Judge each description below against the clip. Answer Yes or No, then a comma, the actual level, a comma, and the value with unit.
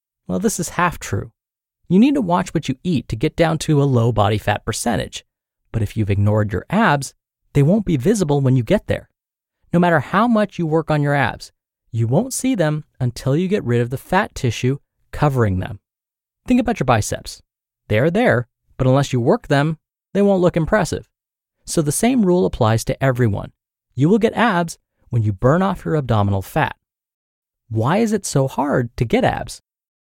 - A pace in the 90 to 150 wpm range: No, average, 200 wpm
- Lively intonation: Yes, wide, 6.9 semitones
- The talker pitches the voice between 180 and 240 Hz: No, medium, 140 Hz